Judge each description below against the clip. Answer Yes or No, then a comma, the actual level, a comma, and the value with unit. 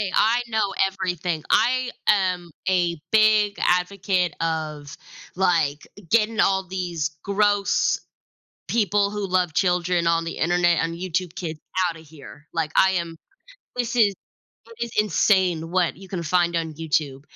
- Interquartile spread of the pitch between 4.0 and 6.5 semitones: No, average, 3.4 semitones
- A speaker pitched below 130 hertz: No, medium, 180 Hz